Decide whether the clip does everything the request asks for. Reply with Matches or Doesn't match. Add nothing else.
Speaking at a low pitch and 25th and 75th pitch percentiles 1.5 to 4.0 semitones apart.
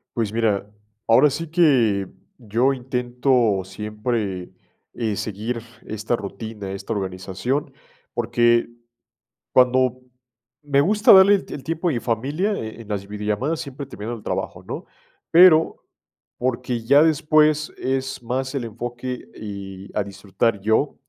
Doesn't match